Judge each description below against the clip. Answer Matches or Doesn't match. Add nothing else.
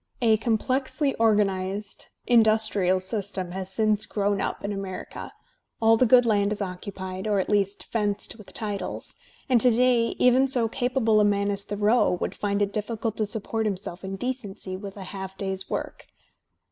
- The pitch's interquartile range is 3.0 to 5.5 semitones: Doesn't match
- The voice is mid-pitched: Doesn't match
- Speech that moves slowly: Doesn't match